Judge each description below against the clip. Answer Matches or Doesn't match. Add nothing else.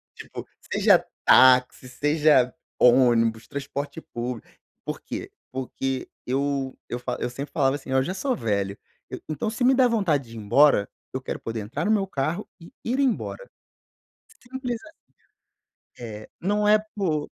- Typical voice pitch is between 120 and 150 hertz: Matches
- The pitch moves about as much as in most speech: Doesn't match